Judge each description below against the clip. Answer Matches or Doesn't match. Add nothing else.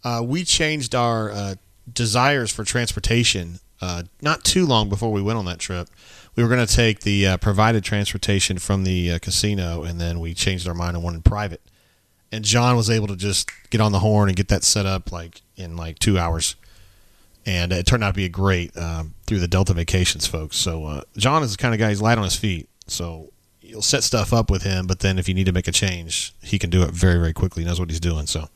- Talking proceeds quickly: Matches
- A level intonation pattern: Doesn't match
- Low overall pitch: Matches